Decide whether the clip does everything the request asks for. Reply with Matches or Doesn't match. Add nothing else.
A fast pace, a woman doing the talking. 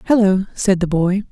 Doesn't match